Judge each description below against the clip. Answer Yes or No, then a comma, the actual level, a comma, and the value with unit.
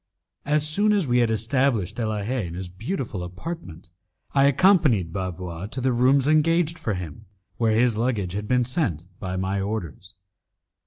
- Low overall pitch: Yes, low, 115 Hz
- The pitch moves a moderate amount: No, wide, 6.8 semitones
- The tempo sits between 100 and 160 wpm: No, average, 170 wpm